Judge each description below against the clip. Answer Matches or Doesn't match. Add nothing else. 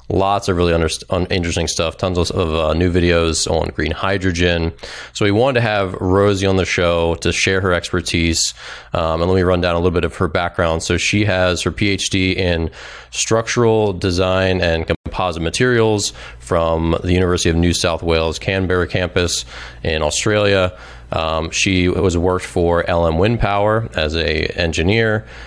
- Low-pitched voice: Matches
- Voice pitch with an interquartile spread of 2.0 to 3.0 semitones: Matches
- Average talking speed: Matches